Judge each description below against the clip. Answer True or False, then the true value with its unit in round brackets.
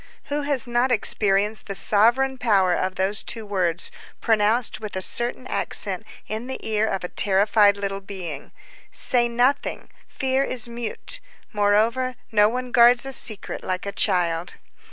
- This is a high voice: True (215 Hz)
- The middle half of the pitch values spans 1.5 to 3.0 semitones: False (3.8 semitones)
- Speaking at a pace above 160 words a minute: False (155 wpm)